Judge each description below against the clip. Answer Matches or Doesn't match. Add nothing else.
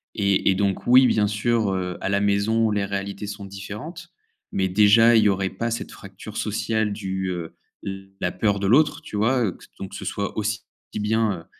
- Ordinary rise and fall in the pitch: Doesn't match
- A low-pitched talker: Matches